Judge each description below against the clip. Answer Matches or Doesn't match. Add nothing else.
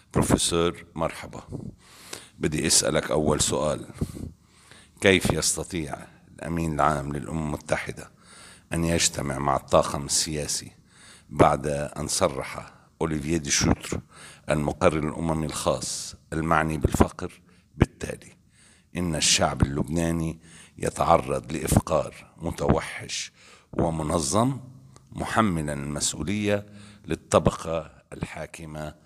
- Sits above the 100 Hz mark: Doesn't match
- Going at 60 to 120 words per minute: Matches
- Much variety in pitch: Doesn't match